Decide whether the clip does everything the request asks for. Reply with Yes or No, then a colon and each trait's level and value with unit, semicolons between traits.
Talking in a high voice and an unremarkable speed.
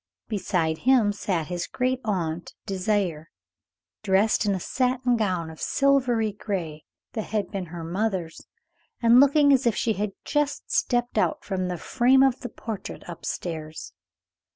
Yes: high, 205 Hz; average, 155 wpm